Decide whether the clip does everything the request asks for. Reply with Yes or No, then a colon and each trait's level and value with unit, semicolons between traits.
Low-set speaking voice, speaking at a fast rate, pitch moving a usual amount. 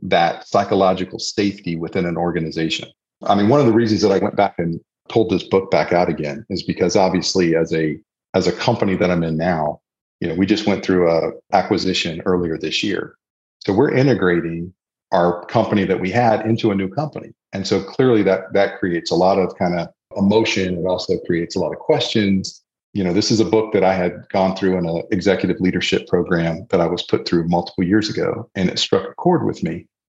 Yes: very low, 90 Hz; fast, 215 wpm; average, 3.1 semitones